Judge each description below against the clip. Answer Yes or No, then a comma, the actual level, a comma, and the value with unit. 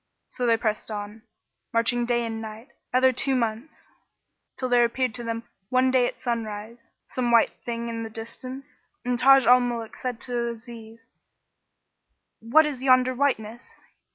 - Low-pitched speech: No, high, 235 Hz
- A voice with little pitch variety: Yes, narrow, 1.9 semitones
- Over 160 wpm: No, average, 155 wpm